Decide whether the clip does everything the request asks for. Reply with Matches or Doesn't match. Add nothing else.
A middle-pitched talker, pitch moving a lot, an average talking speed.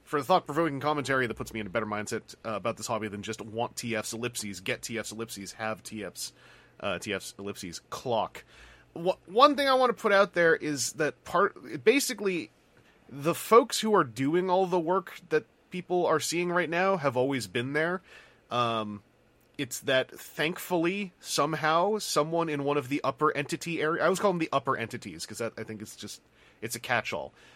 Matches